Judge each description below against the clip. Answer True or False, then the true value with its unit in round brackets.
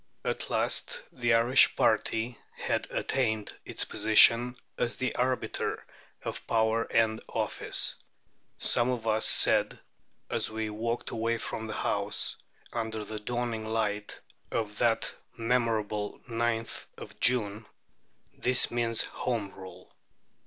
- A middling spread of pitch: False (1.5 semitones)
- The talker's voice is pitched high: False (115 Hz)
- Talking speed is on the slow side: True (120 wpm)